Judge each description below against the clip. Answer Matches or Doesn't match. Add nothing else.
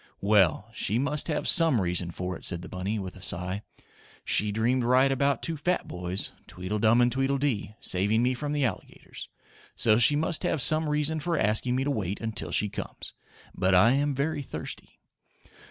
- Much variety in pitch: Matches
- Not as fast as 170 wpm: Doesn't match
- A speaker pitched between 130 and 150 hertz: Doesn't match